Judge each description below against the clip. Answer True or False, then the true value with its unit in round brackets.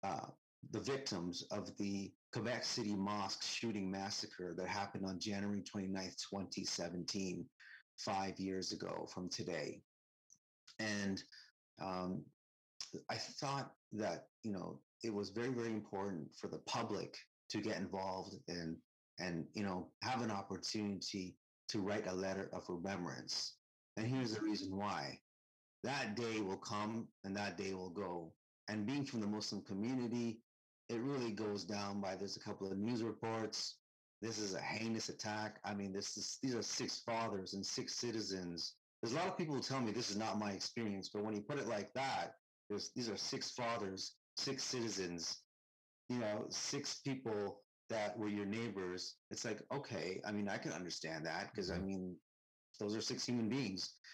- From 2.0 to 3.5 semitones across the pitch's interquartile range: True (2.9 semitones)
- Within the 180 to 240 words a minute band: False (165 wpm)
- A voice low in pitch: True (100 Hz)